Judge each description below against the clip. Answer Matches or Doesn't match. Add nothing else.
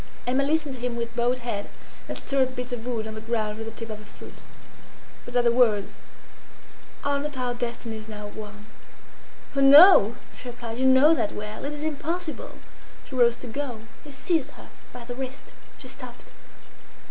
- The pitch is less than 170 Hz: Doesn't match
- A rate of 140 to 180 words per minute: Doesn't match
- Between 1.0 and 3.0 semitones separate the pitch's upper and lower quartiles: Doesn't match